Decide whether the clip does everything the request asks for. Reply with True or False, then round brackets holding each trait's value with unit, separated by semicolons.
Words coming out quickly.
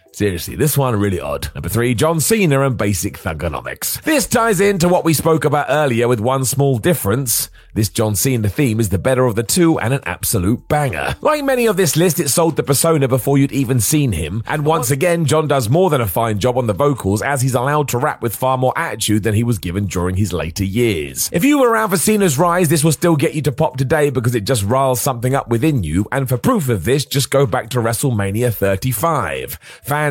True (235 wpm)